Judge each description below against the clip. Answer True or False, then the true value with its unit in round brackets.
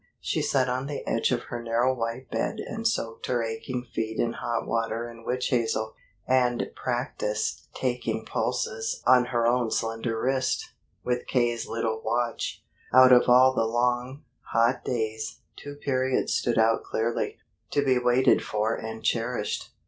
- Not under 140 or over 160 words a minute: True (155 wpm)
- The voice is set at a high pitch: False (120 Hz)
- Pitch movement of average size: False (2.1 semitones)